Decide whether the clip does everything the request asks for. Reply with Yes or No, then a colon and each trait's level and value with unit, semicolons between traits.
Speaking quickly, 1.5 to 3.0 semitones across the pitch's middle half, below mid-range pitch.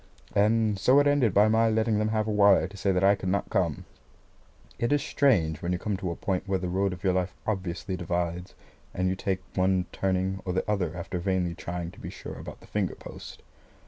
Yes: fast, 230 wpm; average, 2.7 semitones; very low, 95 Hz